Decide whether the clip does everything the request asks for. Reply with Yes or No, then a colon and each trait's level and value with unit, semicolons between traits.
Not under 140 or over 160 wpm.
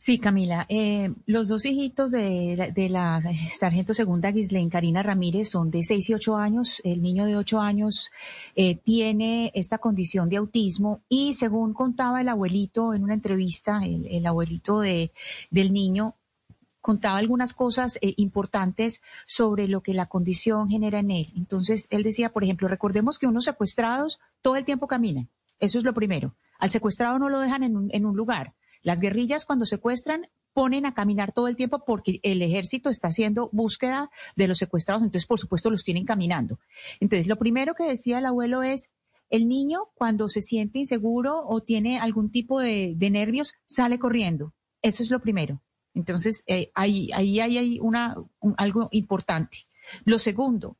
No: average, 175 wpm